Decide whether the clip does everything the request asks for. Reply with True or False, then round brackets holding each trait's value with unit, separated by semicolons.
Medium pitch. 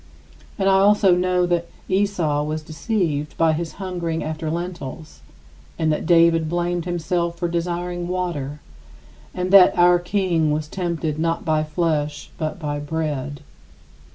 True (170 Hz)